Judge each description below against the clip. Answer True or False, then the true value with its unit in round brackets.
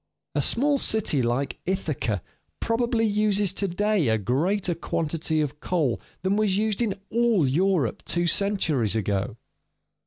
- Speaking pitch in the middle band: True (180 Hz)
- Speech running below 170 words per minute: True (135 wpm)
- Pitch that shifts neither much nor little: False (7.0 semitones)